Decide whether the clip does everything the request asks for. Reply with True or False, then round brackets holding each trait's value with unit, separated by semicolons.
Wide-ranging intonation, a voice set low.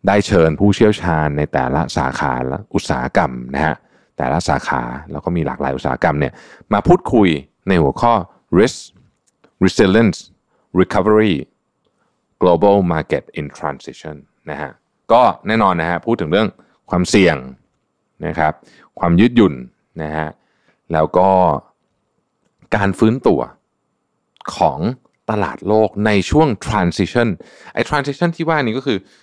True (5.8 semitones; 95 Hz)